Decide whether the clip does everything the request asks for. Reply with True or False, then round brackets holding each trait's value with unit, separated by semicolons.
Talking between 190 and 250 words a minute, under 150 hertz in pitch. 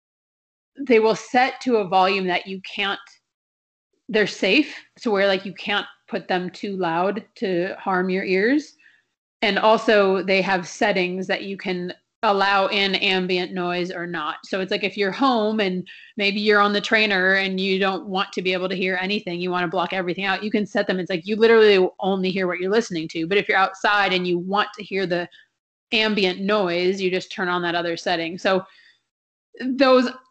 False (200 wpm; 195 Hz)